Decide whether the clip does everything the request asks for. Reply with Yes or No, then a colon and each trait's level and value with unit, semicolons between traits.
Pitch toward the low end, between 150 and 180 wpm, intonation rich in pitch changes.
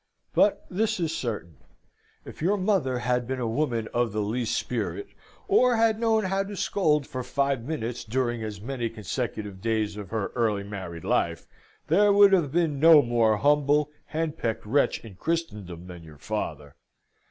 Yes: low, 125 Hz; average, 165 wpm; wide, 7.2 semitones